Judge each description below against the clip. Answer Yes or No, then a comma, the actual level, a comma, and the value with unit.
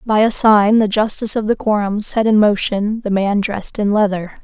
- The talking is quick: Yes, fast, 215 wpm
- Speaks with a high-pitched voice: Yes, high, 210 Hz